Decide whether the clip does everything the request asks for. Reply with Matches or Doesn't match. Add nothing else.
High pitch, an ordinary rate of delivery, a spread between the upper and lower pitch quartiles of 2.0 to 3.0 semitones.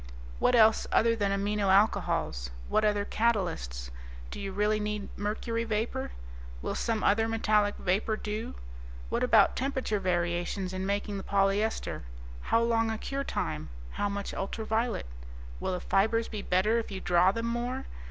Matches